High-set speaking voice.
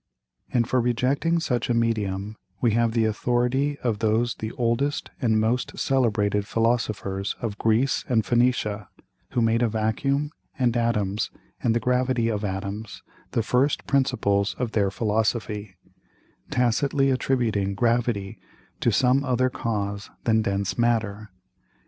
No: low, 115 Hz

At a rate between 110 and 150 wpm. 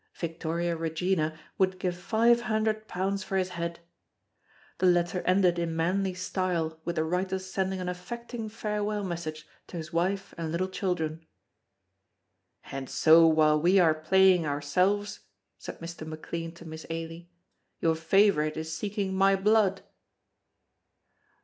Yes: slow, 135 wpm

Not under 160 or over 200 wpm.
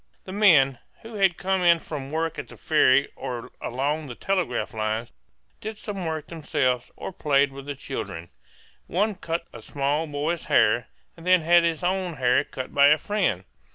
Yes: average, 180 wpm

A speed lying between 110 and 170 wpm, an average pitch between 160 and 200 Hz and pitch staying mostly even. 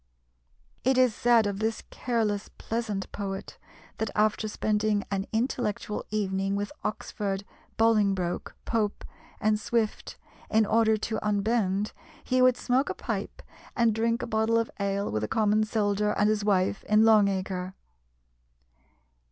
No: average, 140 wpm; high, 215 Hz; narrow, 1.9 semitones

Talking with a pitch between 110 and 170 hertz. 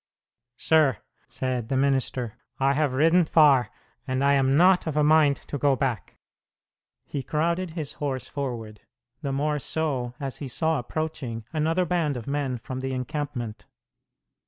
Yes: medium, 140 Hz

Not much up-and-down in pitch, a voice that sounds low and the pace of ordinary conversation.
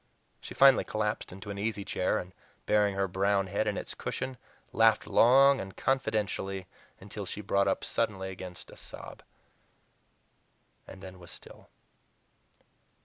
Yes: narrow, 2.2 semitones; low, 100 Hz; average, 145 wpm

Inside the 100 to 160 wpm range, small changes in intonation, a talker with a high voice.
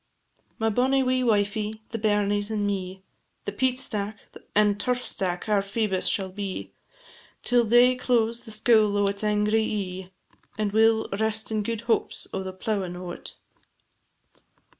Yes: average, 155 wpm; narrow, 2.1 semitones; high, 210 Hz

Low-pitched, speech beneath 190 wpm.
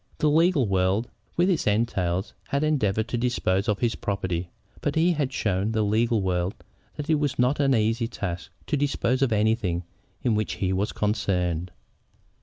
Yes: low, 110 Hz; average, 175 wpm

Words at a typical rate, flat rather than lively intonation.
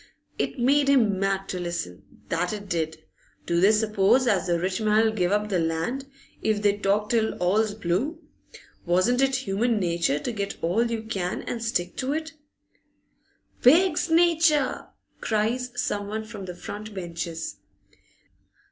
No: average, 155 wpm; average, 5.0 semitones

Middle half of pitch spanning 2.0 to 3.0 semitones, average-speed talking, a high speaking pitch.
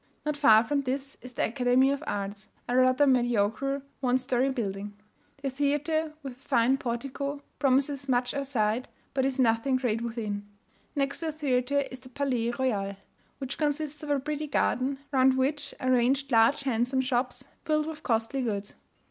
Yes: narrow, 2.6 semitones; average, 170 wpm; very high, 260 Hz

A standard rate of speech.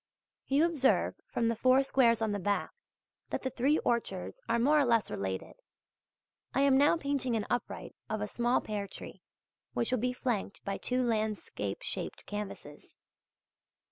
Yes: average, 165 wpm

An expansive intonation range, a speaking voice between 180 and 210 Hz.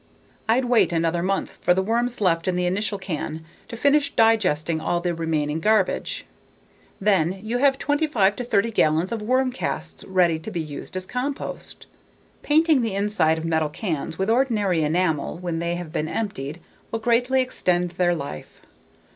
Yes: wide, 5.8 semitones; medium, 185 Hz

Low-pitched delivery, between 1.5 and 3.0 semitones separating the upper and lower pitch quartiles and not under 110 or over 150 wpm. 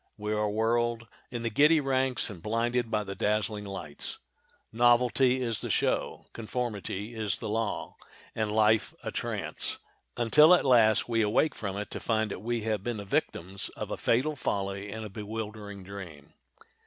No: low, 110 Hz; narrow, 2.5 semitones; average, 165 wpm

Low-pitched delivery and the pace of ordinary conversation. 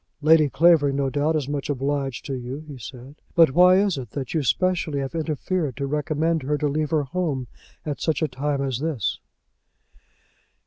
No: medium, 145 Hz; average, 185 wpm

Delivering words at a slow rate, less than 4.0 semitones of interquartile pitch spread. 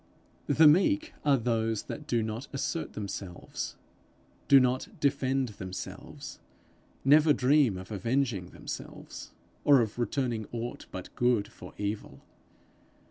No: slow, 120 wpm; average, 4.6 semitones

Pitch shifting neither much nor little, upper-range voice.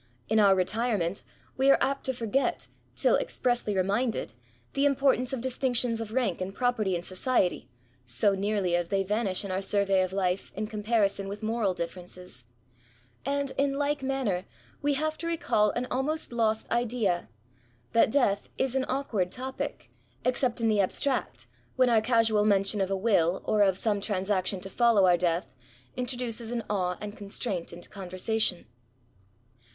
Yes: average, 4.5 semitones; high, 215 Hz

